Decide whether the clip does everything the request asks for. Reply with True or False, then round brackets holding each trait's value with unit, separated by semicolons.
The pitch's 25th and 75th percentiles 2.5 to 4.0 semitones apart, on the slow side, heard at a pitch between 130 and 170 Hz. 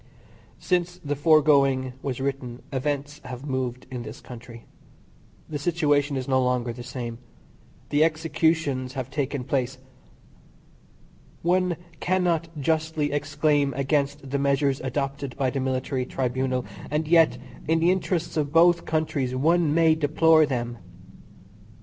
True (3.4 semitones; 130 wpm; 140 Hz)